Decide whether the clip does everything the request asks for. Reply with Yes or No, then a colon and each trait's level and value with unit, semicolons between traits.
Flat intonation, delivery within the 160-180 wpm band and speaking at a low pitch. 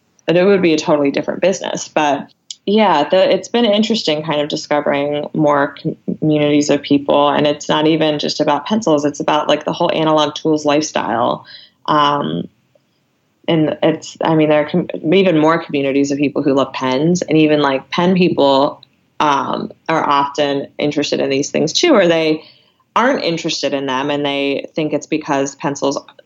No: narrow, 2.2 semitones; average, 175 wpm; medium, 150 Hz